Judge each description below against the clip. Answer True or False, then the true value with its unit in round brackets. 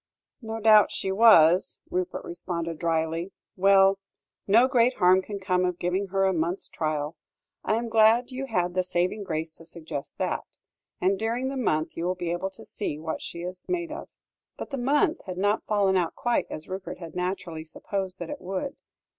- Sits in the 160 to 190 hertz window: True (185 Hz)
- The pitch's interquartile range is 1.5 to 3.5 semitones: False (4.1 semitones)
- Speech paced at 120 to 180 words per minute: False (190 wpm)